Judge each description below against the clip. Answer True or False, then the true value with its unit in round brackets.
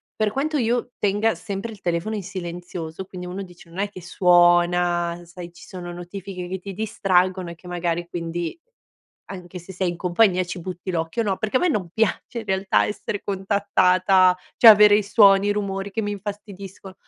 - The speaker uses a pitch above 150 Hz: True (190 Hz)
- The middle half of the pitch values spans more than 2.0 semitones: True (2.6 semitones)